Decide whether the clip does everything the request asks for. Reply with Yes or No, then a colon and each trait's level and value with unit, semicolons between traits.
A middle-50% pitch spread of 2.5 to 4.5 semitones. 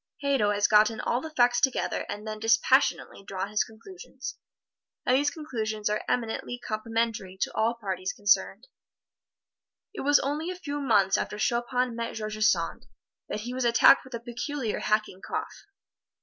Yes: average, 3.4 semitones